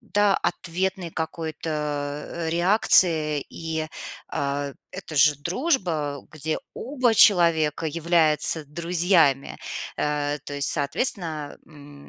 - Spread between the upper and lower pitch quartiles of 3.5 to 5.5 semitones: No, average, 2.9 semitones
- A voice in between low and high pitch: Yes, medium, 160 Hz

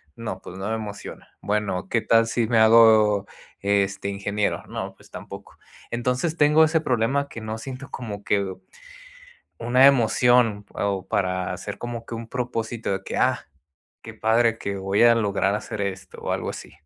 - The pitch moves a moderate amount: Yes, average, 3.1 semitones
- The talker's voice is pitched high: No, low, 110 Hz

